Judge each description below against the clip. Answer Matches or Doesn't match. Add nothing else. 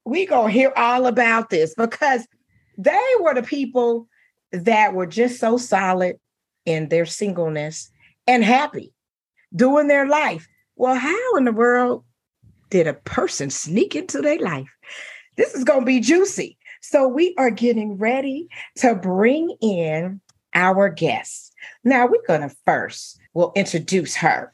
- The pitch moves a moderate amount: Doesn't match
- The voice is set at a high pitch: Matches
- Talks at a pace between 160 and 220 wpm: Doesn't match